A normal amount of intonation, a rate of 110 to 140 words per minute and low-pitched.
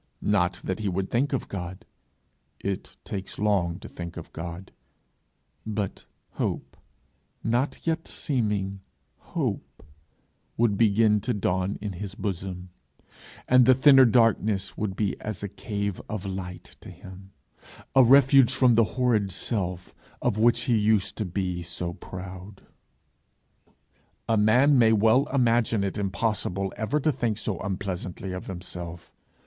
Yes: average, 3.7 semitones; slow, 135 wpm; low, 105 Hz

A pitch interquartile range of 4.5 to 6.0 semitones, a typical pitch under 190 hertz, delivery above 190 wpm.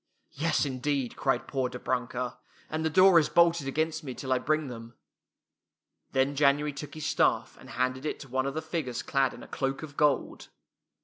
No: average, 3.1 semitones; medium, 140 Hz; average, 200 wpm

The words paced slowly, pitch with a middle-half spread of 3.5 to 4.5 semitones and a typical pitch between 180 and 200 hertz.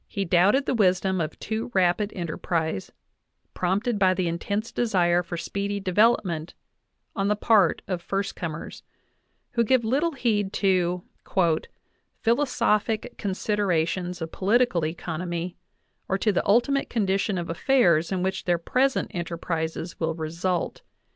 Yes: slow, 130 wpm; average, 3.8 semitones; high, 190 Hz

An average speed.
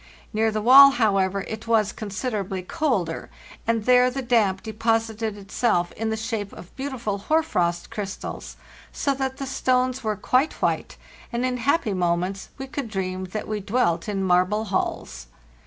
Yes: average, 165 wpm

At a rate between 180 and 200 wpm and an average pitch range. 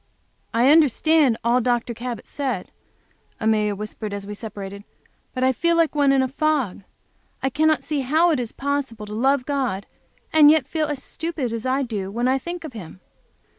Yes: average, 185 wpm; average, 4.9 semitones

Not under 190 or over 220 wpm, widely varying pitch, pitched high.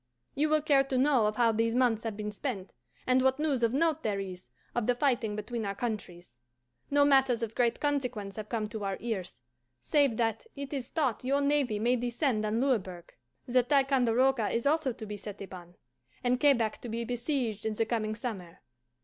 No: average, 200 wpm; average, 4.0 semitones; high, 235 Hz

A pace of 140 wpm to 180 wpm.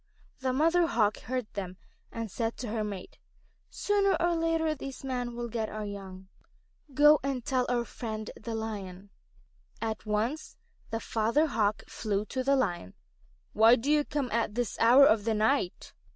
Yes: average, 170 wpm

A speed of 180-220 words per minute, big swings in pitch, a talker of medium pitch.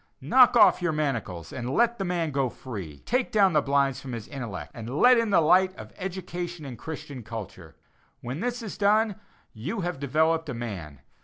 Yes: average, 190 wpm; wide, 7.5 semitones; medium, 150 Hz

